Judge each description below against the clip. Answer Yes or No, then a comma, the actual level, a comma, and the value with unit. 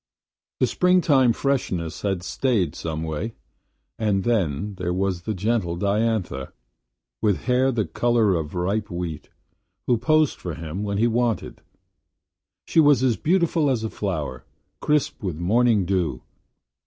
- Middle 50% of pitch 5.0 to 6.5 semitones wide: Yes, wide, 5.6 semitones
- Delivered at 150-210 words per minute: No, average, 140 wpm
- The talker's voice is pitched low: Yes, low, 105 Hz